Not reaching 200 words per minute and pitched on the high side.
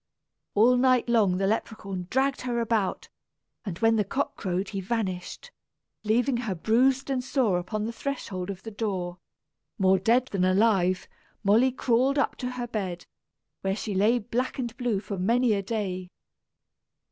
Yes: average, 160 wpm; high, 220 Hz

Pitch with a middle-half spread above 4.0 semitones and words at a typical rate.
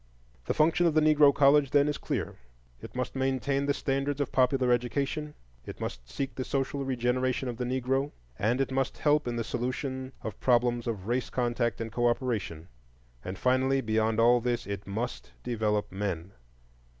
No: average, 2.7 semitones; average, 175 wpm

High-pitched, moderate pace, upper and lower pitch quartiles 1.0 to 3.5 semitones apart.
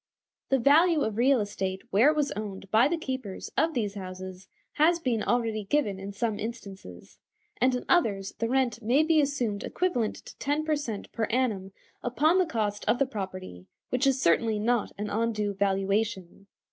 No: high, 225 Hz; average, 180 wpm; average, 5.2 semitones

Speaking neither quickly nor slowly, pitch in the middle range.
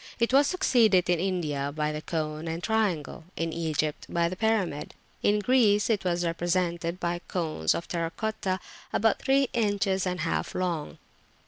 Yes: average, 165 wpm; medium, 180 Hz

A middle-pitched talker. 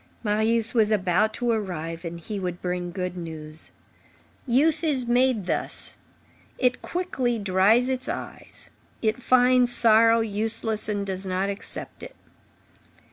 No: high, 215 Hz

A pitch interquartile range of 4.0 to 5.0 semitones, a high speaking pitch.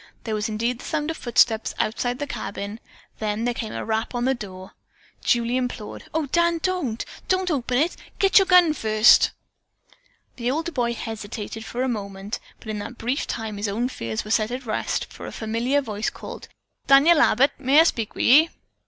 Yes: average, 4.6 semitones; high, 240 Hz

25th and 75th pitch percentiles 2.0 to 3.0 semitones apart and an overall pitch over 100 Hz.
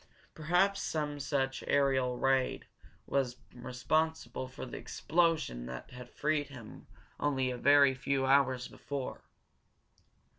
Yes: narrow, 2.5 semitones; low, 135 Hz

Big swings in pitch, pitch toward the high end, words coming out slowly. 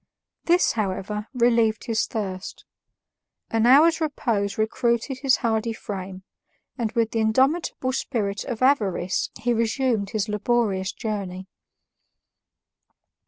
No: average, 3.5 semitones; high, 225 Hz; slow, 110 wpm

